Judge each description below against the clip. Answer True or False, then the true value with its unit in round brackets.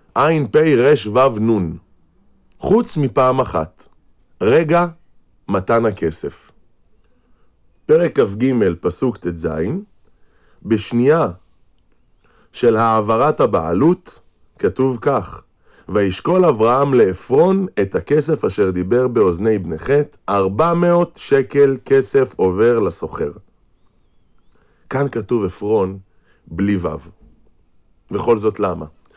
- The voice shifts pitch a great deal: True (7.1 semitones)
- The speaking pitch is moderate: False (115 Hz)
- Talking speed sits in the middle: False (90 wpm)